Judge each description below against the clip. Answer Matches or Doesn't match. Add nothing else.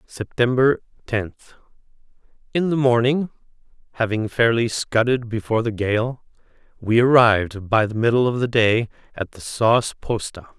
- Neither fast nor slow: Doesn't match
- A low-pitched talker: Matches